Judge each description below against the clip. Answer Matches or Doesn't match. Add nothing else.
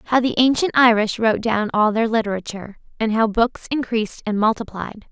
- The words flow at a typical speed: Matches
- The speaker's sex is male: Doesn't match